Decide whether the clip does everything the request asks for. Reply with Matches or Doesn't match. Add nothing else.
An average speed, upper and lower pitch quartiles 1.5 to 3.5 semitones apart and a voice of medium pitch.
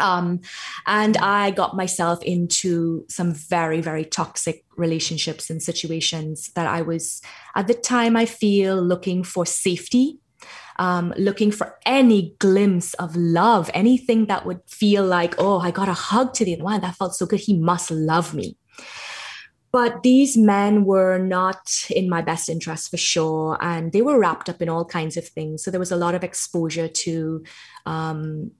Matches